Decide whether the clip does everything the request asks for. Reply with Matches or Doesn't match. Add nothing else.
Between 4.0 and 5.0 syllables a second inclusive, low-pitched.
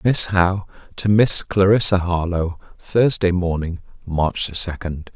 Matches